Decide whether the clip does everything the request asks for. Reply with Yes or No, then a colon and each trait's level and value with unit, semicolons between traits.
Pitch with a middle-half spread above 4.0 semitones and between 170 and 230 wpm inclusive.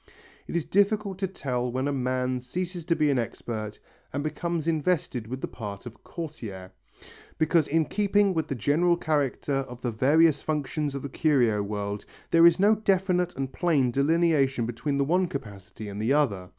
Yes: average, 5.3 semitones; average, 180 wpm